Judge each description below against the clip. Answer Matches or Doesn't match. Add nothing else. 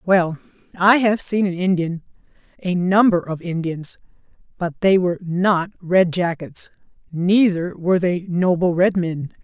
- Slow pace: Matches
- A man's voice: Doesn't match